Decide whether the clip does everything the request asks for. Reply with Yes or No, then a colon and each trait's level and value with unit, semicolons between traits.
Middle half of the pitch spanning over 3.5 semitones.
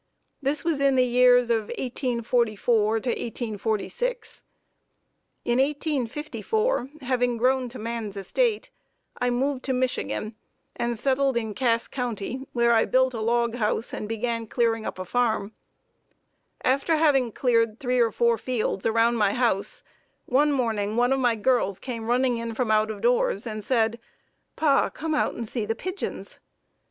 No: average, 2.7 semitones